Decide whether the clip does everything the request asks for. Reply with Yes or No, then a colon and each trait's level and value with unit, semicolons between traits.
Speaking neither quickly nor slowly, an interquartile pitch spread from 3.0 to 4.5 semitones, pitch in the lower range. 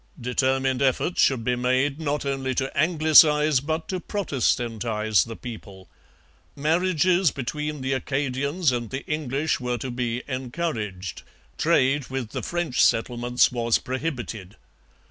No: slow, 125 wpm; average, 3.7 semitones; low, 130 Hz